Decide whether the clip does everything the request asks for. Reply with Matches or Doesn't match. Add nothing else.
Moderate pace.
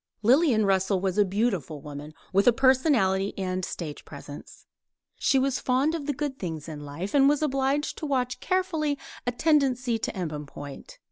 Matches